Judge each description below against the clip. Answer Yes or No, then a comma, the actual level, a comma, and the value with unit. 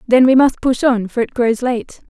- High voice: Yes, high, 245 Hz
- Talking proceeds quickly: Yes, fast, 255 wpm